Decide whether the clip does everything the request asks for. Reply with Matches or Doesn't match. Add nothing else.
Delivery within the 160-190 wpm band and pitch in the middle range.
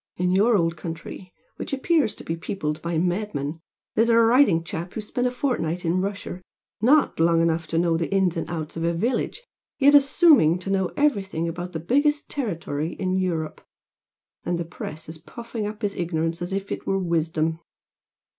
Matches